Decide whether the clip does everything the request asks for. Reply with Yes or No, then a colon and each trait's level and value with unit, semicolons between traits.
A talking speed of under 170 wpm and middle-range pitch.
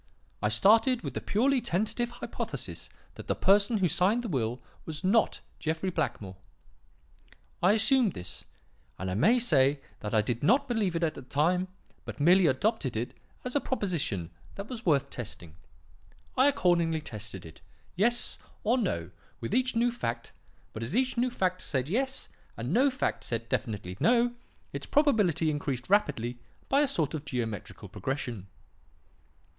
Yes: average, 160 wpm; medium, 170 Hz